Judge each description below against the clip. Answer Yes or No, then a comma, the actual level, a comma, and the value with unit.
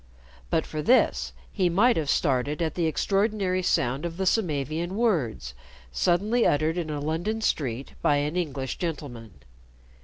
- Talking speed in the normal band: Yes, average, 150 wpm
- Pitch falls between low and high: Yes, medium, 160 Hz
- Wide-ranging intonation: No, average, 4.6 semitones